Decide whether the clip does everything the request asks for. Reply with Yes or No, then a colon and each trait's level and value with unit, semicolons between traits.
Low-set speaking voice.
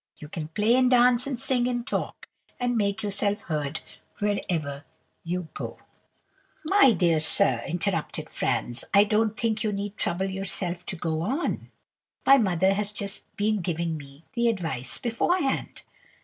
No: high, 200 Hz